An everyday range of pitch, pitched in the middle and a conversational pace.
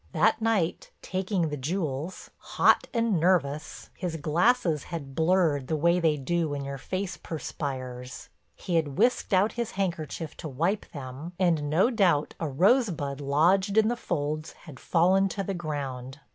Yes: average, 4.7 semitones; medium, 165 Hz; average, 160 wpm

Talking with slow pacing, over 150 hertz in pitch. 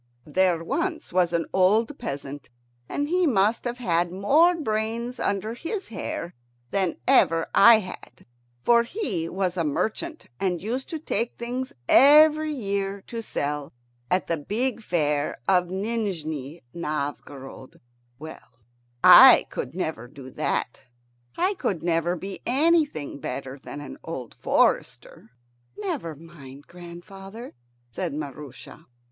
Yes: slow, 130 wpm; high, 190 Hz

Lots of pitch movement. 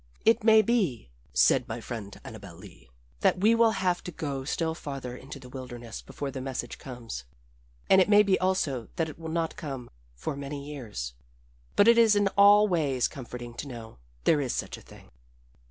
Yes: wide, 7.4 semitones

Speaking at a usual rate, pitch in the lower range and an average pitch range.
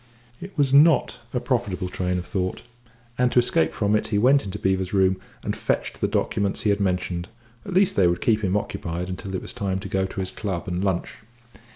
No: fast, 220 wpm; very low, 95 Hz; average, 3.5 semitones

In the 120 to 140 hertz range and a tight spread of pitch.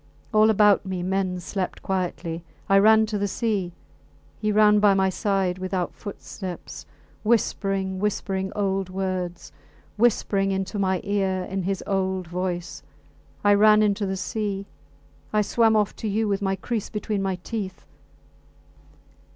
No: high, 195 Hz; narrow, 1.9 semitones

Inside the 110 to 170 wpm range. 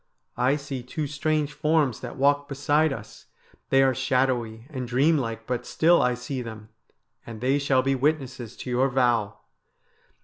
Yes: average, 165 wpm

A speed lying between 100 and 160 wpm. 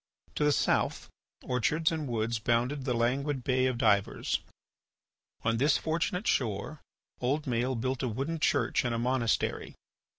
Yes: average, 145 wpm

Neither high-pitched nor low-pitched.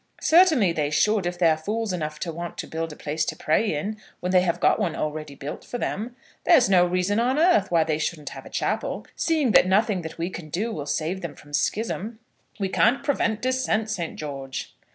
Yes: medium, 180 Hz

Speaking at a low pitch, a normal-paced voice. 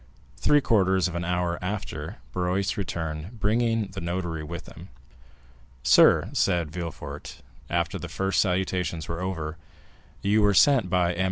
Yes: very low, 90 Hz; average, 150 wpm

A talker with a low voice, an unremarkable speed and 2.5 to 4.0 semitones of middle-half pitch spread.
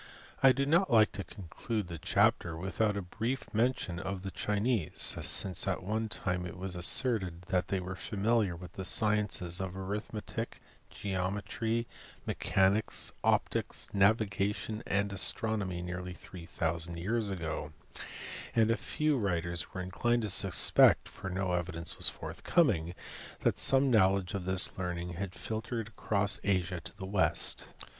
Yes: very low, 95 Hz; average, 150 wpm; average, 3.4 semitones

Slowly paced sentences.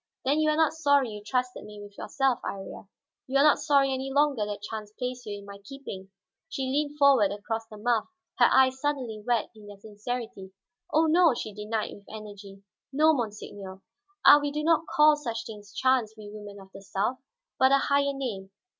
No: average, 200 wpm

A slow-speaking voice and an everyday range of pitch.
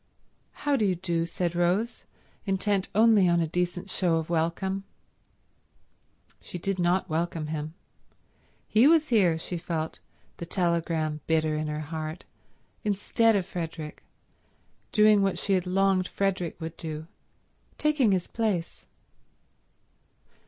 Yes: slow, 130 wpm; average, 3.2 semitones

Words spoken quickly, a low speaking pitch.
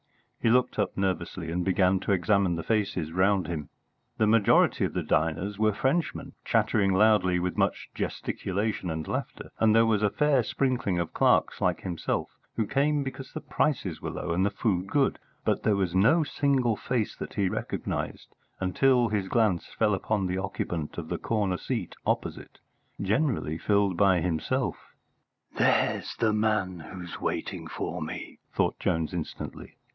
No: average, 165 wpm; low, 100 Hz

